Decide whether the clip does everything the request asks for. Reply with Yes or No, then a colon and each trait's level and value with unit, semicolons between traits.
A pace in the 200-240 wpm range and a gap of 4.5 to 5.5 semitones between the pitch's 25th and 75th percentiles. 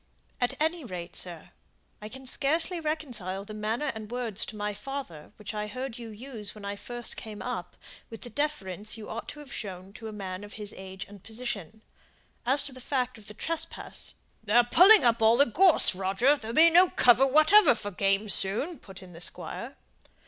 Yes: fast, 205 wpm; average, 5.0 semitones